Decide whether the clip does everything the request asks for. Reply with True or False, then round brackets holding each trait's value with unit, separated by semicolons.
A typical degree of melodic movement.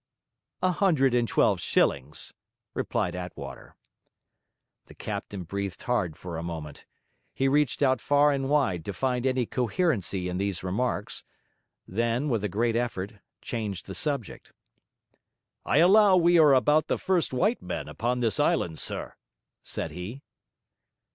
False (7.2 semitones)